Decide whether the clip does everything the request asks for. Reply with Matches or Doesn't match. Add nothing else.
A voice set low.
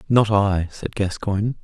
Matches